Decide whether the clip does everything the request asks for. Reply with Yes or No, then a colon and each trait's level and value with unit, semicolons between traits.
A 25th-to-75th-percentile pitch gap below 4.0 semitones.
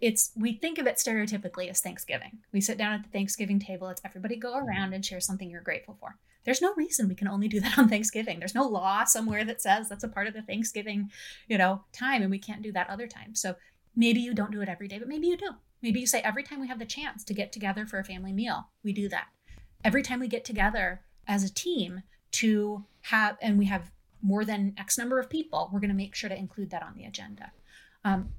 Yes: average, 3.1 semitones